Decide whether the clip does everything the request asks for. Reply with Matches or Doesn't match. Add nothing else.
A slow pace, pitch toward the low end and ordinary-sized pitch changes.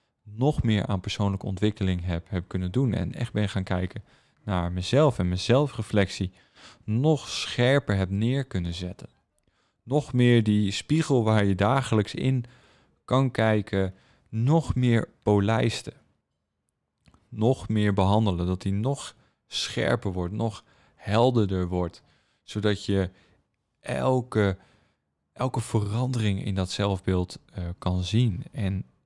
Matches